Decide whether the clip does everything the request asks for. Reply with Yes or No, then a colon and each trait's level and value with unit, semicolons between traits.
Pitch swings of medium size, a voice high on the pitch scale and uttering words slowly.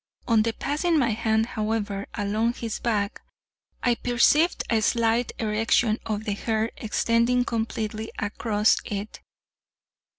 No: narrow, 1.7 semitones; high, 225 Hz; slow, 120 wpm